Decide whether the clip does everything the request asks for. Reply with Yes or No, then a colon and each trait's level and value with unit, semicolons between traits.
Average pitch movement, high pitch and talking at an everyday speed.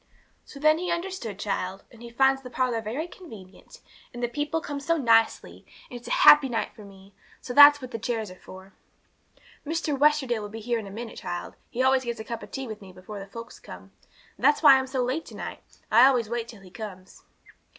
No: average, 4.5 semitones; high, 240 Hz; fast, 225 wpm